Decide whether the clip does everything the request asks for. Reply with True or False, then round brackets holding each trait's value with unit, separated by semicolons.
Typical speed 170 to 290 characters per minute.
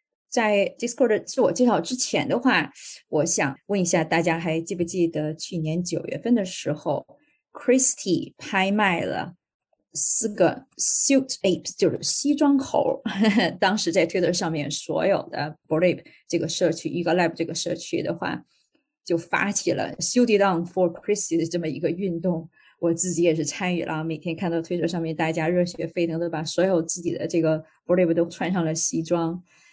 False (365 characters per minute)